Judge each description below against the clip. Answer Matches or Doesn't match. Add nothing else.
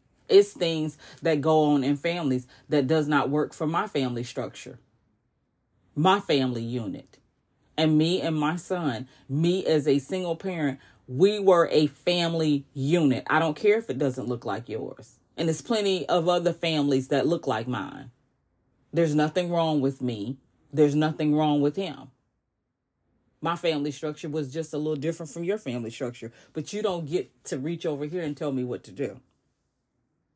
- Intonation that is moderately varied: Matches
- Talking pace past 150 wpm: Matches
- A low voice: Doesn't match